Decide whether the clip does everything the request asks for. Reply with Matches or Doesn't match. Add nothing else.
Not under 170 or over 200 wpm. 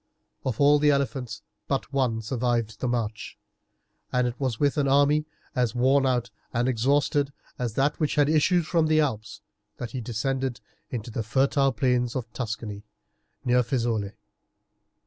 Doesn't match